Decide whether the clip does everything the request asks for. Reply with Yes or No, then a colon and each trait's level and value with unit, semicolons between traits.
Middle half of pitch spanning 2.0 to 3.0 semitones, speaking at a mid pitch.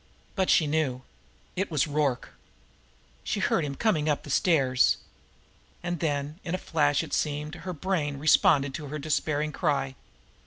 Yes: narrow, 2.5 semitones; medium, 150 Hz